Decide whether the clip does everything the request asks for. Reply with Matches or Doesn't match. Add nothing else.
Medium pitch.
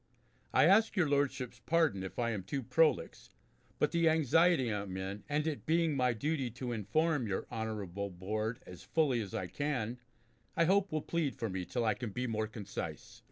Doesn't match